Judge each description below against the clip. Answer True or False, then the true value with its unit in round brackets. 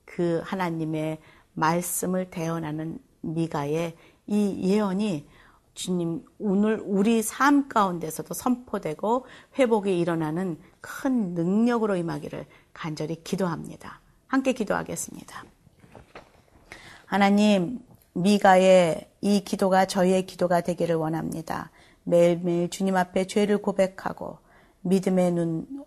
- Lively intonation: False (3.7 semitones)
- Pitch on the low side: False (185 Hz)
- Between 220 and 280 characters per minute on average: True (255 characters per minute)